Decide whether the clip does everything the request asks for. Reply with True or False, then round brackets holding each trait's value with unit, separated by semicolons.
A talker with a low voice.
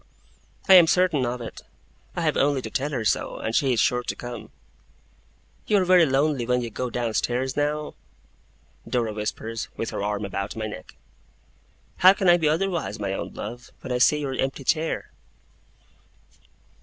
True (130 Hz)